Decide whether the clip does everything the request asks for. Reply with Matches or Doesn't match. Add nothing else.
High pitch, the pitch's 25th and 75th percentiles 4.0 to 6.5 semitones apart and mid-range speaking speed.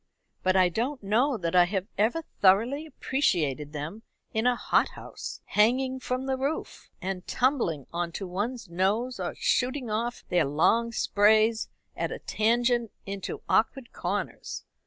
Matches